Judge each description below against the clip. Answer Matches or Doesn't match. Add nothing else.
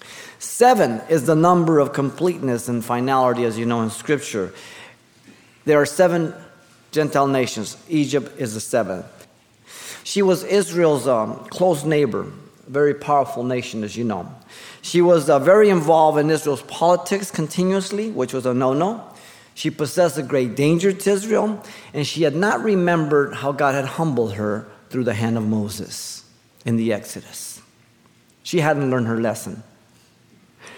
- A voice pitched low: Doesn't match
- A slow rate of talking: Doesn't match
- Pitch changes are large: Matches